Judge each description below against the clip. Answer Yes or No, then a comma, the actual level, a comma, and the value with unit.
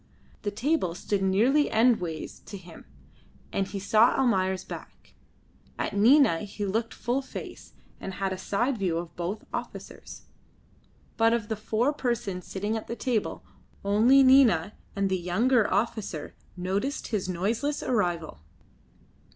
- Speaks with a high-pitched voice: Yes, high, 210 Hz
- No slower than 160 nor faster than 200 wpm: No, average, 140 wpm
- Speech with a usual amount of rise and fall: Yes, average, 4.1 semitones